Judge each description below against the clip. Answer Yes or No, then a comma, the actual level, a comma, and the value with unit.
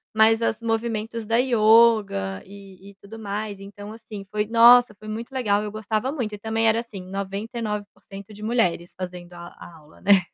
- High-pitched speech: Yes, high, 210 Hz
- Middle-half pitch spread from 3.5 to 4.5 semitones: No, narrow, 2.4 semitones